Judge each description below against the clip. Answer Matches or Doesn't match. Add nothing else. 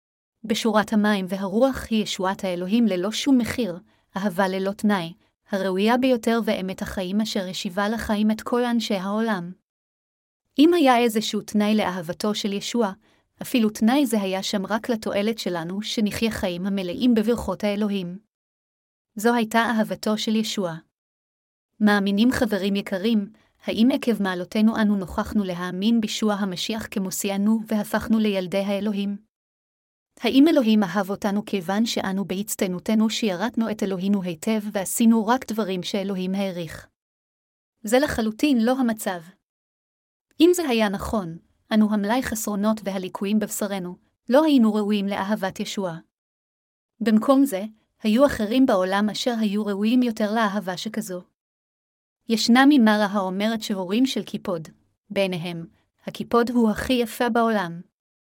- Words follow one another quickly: Doesn't match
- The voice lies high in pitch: Matches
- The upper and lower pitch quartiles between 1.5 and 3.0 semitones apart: Matches